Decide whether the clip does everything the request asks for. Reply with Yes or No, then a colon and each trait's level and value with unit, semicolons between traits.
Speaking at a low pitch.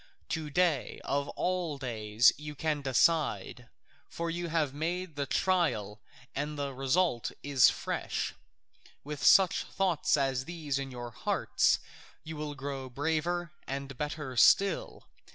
No: medium, 145 Hz